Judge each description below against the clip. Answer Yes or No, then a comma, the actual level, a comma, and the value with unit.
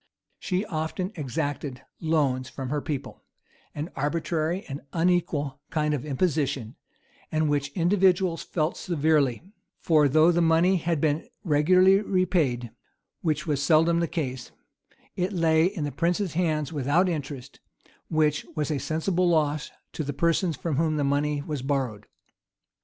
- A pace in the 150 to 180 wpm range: No, average, 140 wpm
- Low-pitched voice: No, medium, 155 Hz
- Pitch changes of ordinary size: Yes, average, 3.0 semitones